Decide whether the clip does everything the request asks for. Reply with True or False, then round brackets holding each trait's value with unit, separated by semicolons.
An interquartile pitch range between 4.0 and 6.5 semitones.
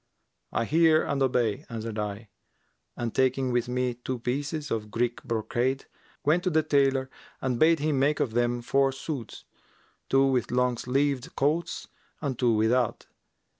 False (2.9 semitones)